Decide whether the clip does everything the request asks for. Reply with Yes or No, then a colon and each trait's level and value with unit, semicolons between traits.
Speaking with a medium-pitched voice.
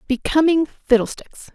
No: very high, 285 Hz